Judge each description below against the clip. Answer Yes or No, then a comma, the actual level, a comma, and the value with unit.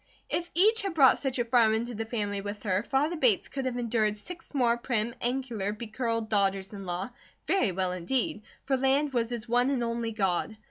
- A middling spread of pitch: Yes, average, 4.0 semitones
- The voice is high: Yes, high, 235 Hz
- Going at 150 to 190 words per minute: No, average, 200 wpm